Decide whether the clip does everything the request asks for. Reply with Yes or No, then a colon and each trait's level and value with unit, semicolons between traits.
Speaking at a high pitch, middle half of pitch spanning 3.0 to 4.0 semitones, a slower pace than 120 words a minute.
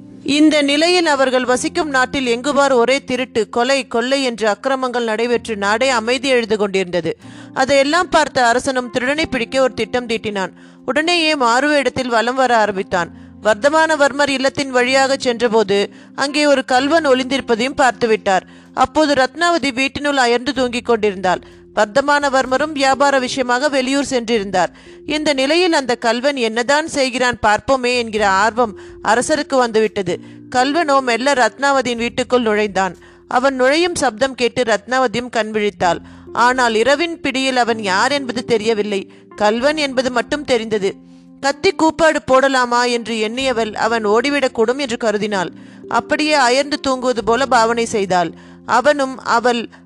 No: very high, 250 Hz; average, 3.6 semitones; average, 125 wpm